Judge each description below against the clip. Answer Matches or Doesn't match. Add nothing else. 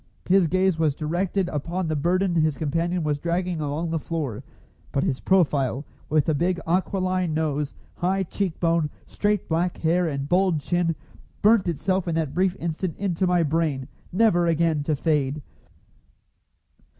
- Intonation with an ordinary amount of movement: Matches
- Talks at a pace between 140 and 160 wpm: Matches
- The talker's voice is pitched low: Doesn't match